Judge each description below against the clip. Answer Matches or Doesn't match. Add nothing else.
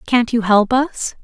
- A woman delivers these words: Matches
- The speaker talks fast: Doesn't match